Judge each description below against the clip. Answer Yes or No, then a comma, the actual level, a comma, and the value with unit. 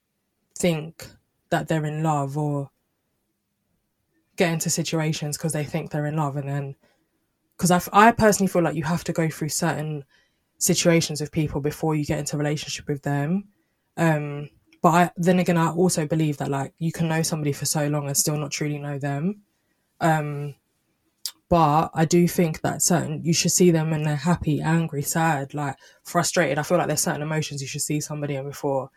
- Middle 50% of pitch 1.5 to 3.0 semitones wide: Yes, average, 2.7 semitones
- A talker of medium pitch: Yes, medium, 155 Hz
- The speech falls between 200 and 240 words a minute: No, average, 190 wpm